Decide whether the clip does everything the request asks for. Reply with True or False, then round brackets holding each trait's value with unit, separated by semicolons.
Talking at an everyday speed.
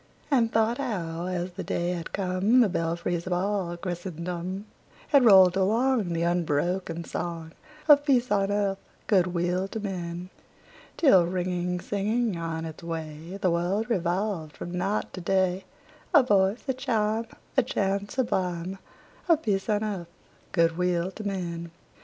True (150 wpm)